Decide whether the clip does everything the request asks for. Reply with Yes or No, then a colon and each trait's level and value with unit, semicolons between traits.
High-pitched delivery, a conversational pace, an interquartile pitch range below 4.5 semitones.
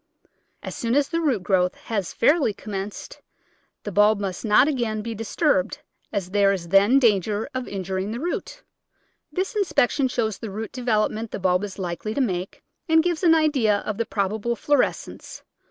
No: high, 215 Hz; average, 175 wpm; average, 4.8 semitones